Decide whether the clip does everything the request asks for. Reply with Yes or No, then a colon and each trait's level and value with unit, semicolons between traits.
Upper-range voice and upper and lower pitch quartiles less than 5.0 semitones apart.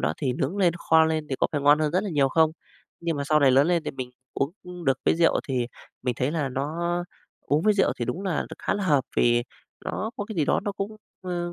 No: medium, 155 Hz; average, 4.6 semitones